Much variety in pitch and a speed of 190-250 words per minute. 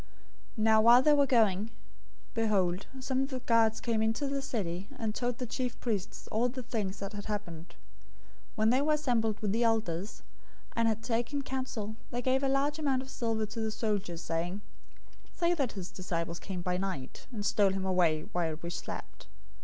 No: average, 4.6 semitones; average, 195 wpm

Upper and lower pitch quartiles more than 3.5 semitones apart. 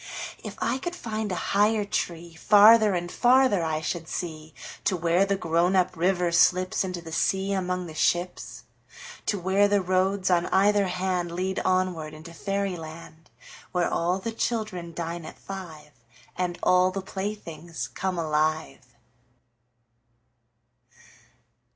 No: average, 2.8 semitones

